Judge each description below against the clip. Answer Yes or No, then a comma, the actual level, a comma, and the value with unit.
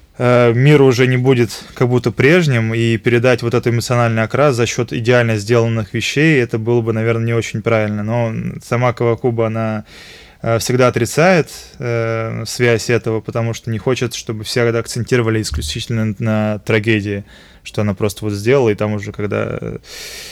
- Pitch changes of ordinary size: No, narrow, 1.9 semitones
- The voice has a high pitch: No, low, 115 Hz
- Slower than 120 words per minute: No, average, 155 wpm